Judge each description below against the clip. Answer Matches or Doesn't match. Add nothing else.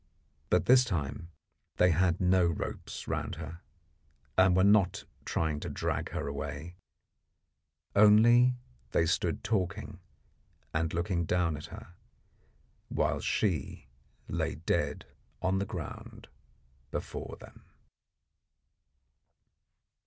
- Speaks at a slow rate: Matches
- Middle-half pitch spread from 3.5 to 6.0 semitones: Doesn't match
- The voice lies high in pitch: Doesn't match